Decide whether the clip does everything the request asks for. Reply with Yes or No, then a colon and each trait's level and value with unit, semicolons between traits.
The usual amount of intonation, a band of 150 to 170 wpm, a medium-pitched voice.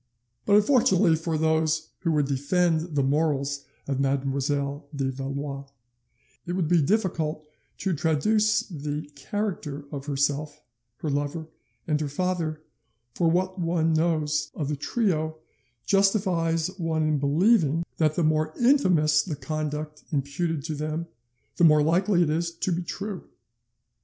No: average, 3.1 semitones; average, 140 wpm; medium, 155 Hz